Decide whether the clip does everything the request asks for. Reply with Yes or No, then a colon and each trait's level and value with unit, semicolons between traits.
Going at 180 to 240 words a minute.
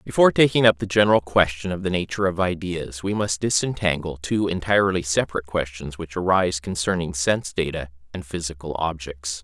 No: average, 165 wpm